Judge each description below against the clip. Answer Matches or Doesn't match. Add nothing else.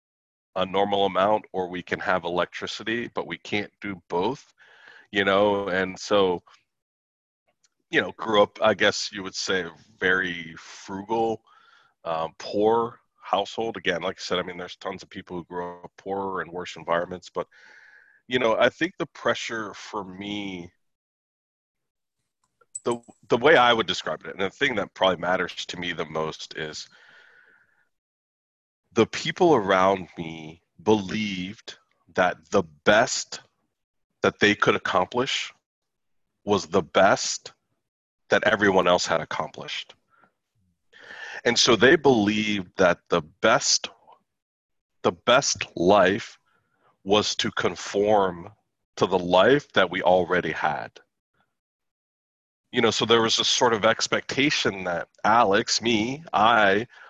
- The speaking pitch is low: Matches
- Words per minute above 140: Doesn't match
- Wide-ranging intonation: Doesn't match